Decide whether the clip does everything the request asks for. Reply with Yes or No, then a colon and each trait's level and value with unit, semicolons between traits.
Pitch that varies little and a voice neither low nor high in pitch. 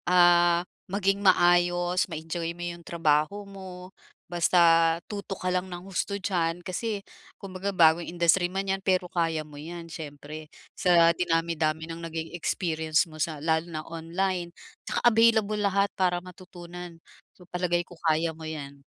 Yes: narrow, 2.1 semitones; medium, 175 Hz